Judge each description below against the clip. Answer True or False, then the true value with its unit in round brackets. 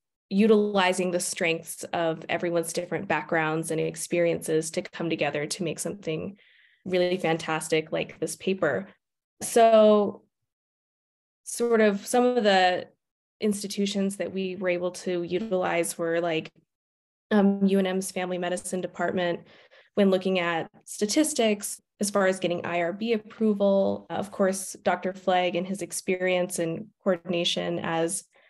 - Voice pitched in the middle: True (180 Hz)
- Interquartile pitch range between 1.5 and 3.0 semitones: True (2.7 semitones)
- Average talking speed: False (125 wpm)